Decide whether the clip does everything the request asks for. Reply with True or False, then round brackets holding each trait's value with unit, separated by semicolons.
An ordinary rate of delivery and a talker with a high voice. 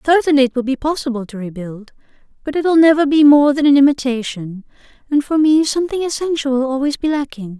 True (195 wpm; 275 Hz)